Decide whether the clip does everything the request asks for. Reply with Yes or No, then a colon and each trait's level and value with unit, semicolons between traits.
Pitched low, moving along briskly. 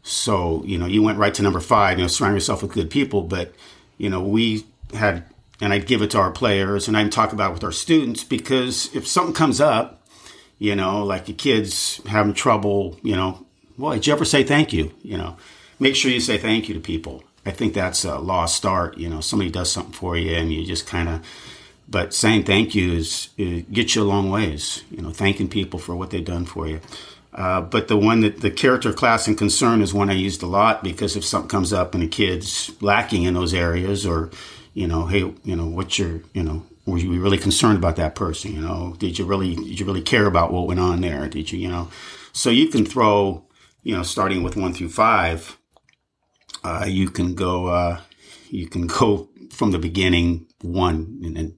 Yes: very low, 95 Hz; fast, 225 wpm